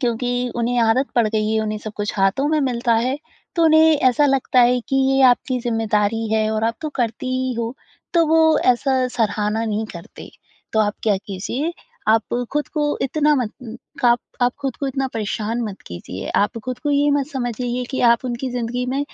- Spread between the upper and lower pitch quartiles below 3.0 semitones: No, average, 3.5 semitones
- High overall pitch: Yes, high, 245 Hz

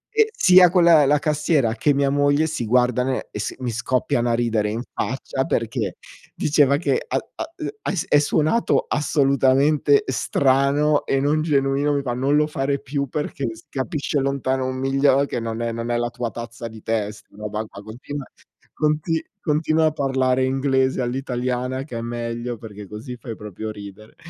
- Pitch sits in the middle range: No, low, 130 Hz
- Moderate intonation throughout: Yes, average, 3.6 semitones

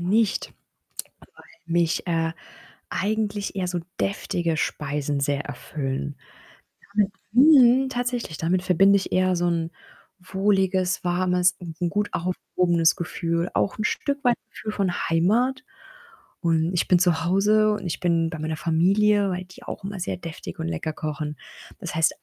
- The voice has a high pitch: No, medium, 180 Hz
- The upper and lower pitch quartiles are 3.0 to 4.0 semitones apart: Yes, average, 3.7 semitones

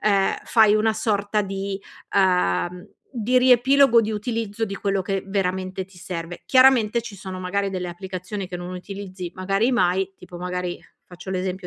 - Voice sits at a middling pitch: No, high, 195 Hz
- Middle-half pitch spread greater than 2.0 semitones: Yes, average, 2.7 semitones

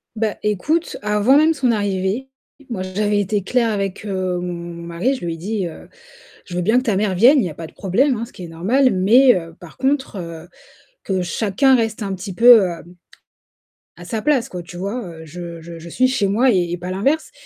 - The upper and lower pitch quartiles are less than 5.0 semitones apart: No, wide, 5.4 semitones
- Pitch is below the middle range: No, high, 200 Hz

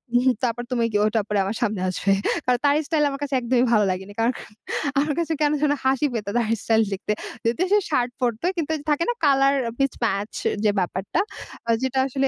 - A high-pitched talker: Yes, high, 245 Hz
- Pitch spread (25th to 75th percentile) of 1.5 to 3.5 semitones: No, average, 4.6 semitones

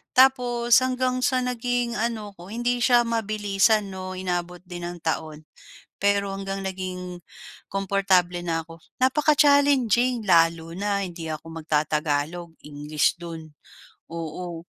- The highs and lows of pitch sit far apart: Yes, wide, 5.9 semitones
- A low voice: No, high, 190 Hz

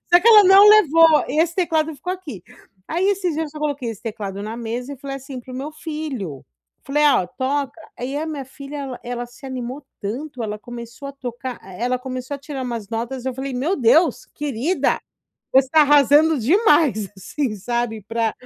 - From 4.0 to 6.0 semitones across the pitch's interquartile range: Yes, average, 4.3 semitones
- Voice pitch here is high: Yes, very high, 270 Hz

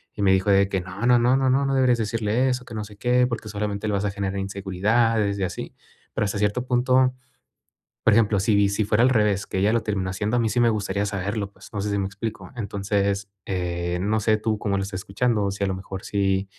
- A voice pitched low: Yes, low, 105 Hz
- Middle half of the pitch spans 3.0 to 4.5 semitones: No, narrow, 2.6 semitones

